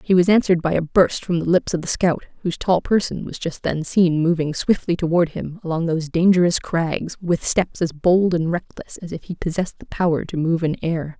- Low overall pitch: No, medium, 170 Hz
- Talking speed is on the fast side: Yes, fast, 230 wpm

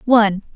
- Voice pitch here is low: No, high, 215 Hz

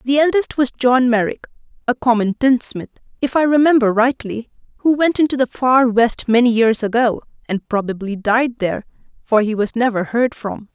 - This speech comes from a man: No, female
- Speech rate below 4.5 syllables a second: No, 5.1 syllables/s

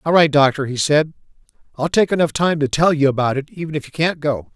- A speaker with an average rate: No, fast, 250 wpm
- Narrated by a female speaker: No, male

